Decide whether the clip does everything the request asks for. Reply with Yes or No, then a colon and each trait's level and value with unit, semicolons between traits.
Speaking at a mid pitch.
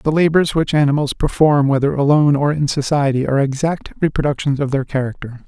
Yes: medium, 145 Hz